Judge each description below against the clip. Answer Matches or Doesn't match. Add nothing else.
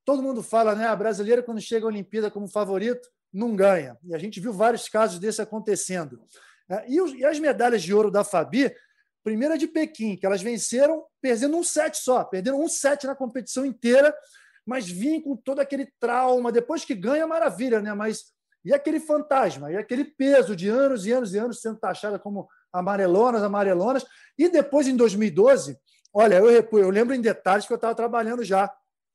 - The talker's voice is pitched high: Matches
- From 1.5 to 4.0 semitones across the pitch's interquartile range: Doesn't match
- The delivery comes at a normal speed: Doesn't match